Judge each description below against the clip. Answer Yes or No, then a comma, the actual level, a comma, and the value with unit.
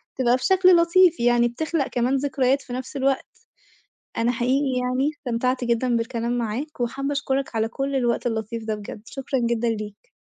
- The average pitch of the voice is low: No, very high, 250 Hz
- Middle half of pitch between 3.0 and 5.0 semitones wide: No, narrow, 2.6 semitones